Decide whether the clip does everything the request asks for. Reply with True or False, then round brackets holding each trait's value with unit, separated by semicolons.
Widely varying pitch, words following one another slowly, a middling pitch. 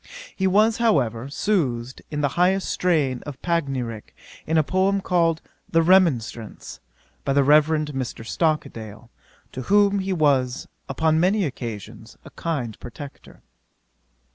True (5.9 semitones; 130 wpm; 155 Hz)